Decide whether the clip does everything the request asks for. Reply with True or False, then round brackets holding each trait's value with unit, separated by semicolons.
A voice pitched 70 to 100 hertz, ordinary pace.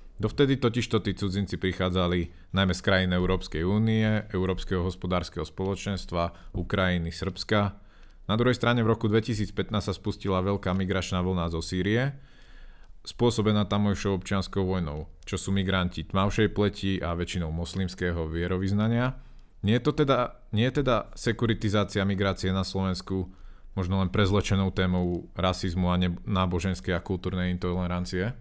True (95 Hz; 135 wpm)